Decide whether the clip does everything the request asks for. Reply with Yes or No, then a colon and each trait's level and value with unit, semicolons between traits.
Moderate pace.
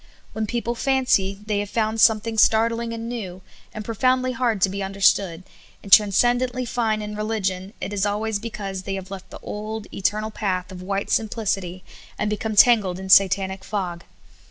Yes: average, 175 wpm